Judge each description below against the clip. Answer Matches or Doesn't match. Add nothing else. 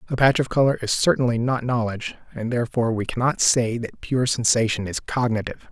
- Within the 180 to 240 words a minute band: Matches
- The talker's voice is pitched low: Matches